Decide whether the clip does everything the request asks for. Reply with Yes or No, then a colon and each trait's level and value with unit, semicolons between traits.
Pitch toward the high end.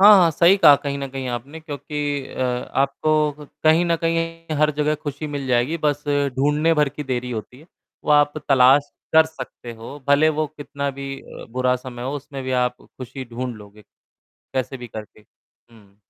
No: medium, 140 Hz